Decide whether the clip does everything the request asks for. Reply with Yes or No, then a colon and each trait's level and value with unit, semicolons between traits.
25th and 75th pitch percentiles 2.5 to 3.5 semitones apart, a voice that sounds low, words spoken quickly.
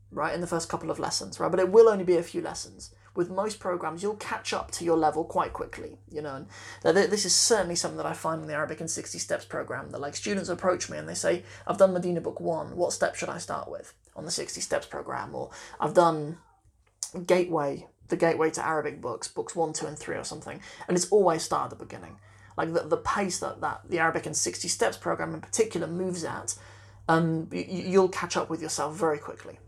No: average, 2.9 semitones; medium, 170 Hz; fast, 235 wpm